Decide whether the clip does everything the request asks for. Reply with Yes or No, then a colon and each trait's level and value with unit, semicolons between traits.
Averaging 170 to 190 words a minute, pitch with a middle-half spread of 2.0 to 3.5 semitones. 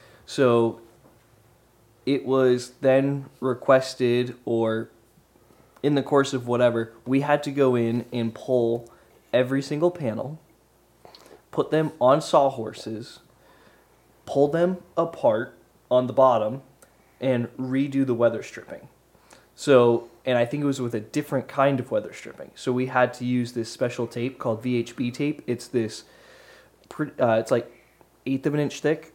No: average, 145 wpm; average, 2.7 semitones